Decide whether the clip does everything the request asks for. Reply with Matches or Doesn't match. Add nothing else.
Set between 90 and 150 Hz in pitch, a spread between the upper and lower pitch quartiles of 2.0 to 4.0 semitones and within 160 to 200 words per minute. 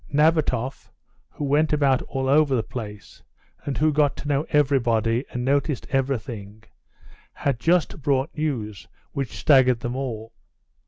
Doesn't match